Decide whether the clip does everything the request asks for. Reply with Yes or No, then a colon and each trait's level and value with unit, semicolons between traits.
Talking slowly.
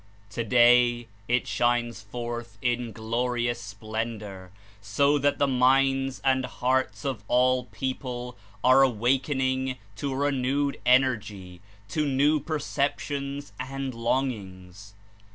Yes: slow, 110 wpm